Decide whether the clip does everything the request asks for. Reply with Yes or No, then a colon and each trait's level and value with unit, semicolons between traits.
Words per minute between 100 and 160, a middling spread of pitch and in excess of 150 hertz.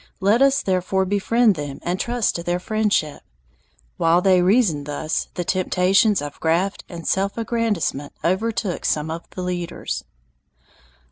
Yes: average, 140 wpm; average, 3.8 semitones; medium, 185 Hz